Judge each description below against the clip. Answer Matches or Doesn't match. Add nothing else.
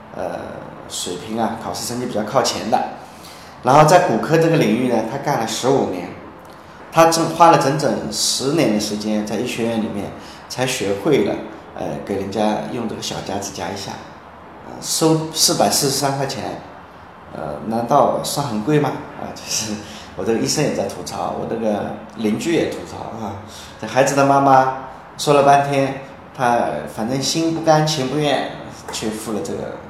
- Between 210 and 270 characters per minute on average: Matches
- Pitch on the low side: Matches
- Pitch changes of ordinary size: Doesn't match